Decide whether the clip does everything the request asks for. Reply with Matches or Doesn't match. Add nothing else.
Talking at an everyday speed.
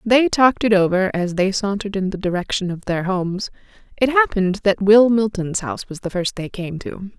Doesn't match